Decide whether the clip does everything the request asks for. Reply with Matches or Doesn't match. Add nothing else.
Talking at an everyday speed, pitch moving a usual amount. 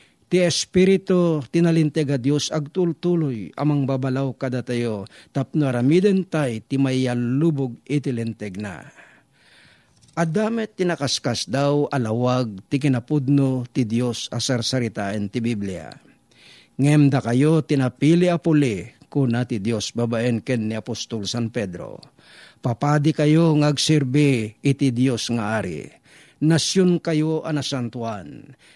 Doesn't match